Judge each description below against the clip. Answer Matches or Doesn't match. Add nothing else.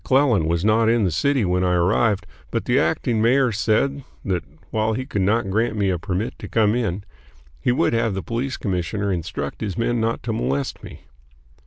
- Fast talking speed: Matches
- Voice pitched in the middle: Doesn't match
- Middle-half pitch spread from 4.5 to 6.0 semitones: Doesn't match